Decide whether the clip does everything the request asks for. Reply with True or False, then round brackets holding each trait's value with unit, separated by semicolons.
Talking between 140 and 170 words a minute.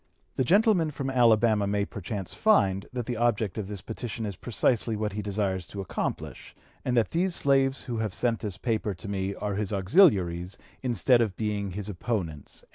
False (185 wpm)